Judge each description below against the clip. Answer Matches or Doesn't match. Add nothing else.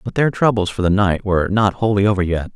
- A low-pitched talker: Matches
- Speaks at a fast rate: Matches